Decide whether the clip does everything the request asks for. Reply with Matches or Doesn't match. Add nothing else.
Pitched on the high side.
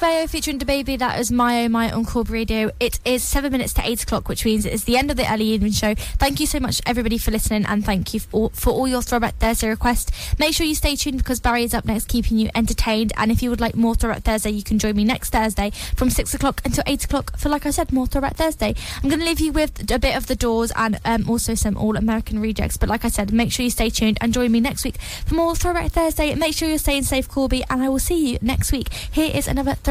Matches